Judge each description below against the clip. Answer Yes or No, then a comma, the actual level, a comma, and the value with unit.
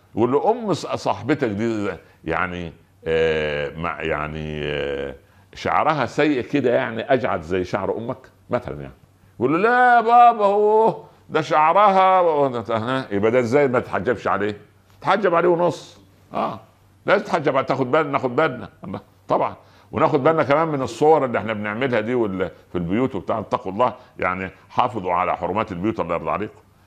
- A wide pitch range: Yes, wide, 8.3 semitones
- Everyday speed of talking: No, fast, 140 wpm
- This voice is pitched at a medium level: No, low, 115 Hz